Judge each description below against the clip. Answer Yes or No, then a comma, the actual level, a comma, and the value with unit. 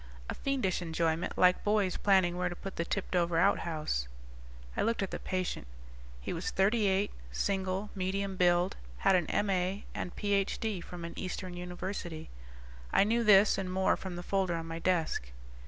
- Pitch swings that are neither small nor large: No, narrow, 2.2 semitones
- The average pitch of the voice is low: No, medium, 185 Hz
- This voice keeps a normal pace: Yes, average, 170 wpm